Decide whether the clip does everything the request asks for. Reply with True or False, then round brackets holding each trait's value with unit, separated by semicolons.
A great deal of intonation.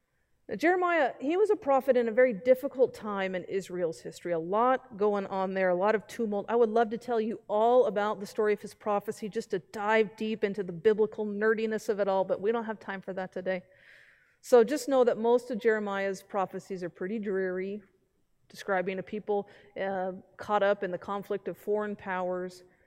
False (3.0 semitones)